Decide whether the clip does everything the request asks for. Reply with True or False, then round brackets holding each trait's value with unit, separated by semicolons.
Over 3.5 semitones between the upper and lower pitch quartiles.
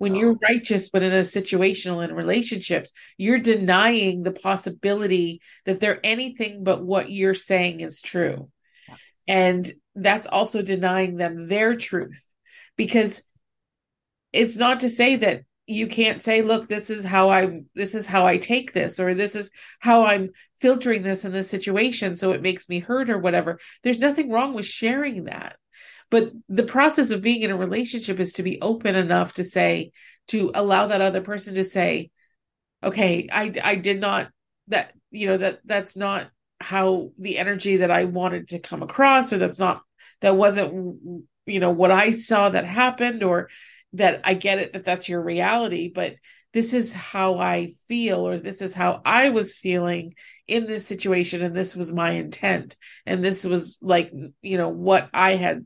False (3.2 semitones)